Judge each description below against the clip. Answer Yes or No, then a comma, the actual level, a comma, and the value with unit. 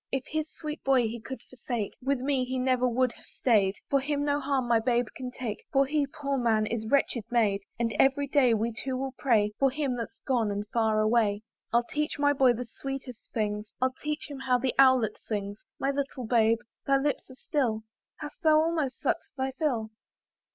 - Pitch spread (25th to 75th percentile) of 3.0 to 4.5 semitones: Yes, average, 3.4 semitones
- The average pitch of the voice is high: Yes, very high, 255 Hz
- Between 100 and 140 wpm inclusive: No, fast, 205 wpm